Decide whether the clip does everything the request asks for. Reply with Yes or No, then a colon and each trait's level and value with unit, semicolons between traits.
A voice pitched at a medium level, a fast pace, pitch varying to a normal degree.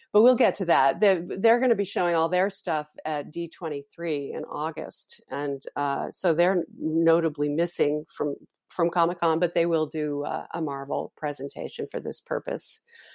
No: medium, 165 Hz; average, 175 wpm; average, 3.2 semitones